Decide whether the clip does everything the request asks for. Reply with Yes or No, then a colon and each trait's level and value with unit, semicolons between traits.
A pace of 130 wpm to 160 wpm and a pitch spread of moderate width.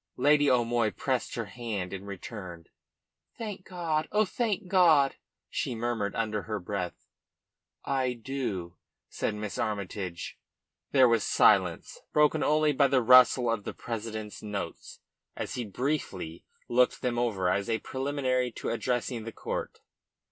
Yes: average, 140 wpm; average, 4.6 semitones